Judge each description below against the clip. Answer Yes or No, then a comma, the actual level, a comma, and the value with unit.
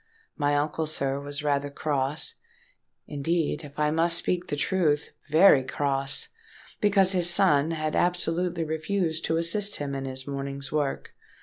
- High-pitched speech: No, medium, 155 Hz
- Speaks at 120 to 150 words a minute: Yes, average, 140 wpm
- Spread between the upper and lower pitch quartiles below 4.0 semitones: Yes, average, 3.5 semitones